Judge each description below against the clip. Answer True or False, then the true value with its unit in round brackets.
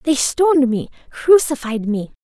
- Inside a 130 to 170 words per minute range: True (135 wpm)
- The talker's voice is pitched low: False (270 Hz)